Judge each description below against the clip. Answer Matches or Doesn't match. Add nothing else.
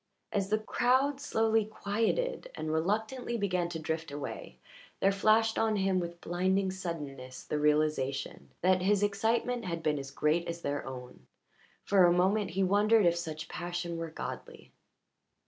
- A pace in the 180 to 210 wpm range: Doesn't match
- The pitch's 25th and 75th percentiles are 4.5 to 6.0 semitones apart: Matches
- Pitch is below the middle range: Doesn't match